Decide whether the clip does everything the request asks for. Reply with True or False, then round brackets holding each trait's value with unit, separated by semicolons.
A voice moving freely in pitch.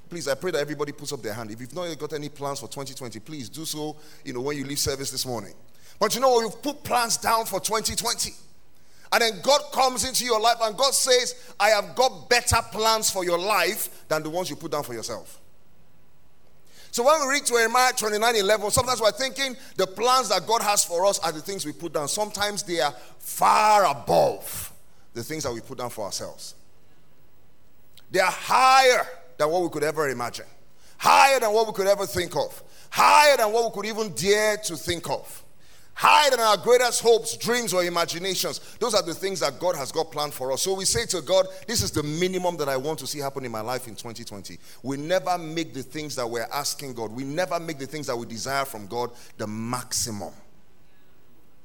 True (8.3 semitones)